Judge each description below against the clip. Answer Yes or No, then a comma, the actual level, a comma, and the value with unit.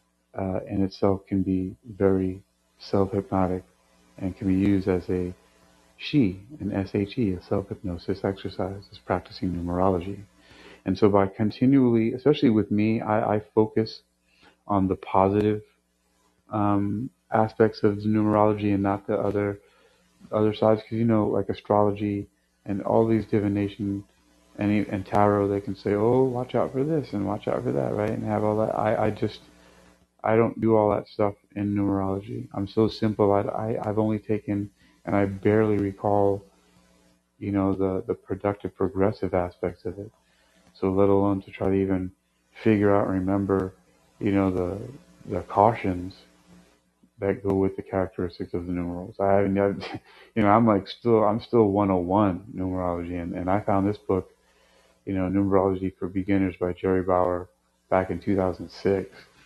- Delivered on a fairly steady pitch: Yes, narrow, 2.2 semitones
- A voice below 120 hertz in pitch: Yes, low, 100 Hz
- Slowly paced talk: No, average, 165 wpm